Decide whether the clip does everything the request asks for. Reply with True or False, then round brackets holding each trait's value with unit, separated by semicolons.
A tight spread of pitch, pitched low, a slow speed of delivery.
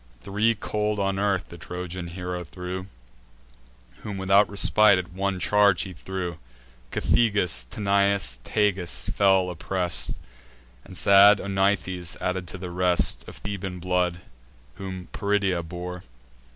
True (1.9 semitones; 95 Hz; 125 wpm)